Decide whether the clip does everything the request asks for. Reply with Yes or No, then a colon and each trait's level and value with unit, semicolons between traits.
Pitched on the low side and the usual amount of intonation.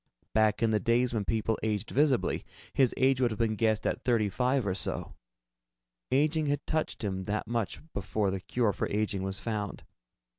Yes: low, 110 Hz; average, 3.4 semitones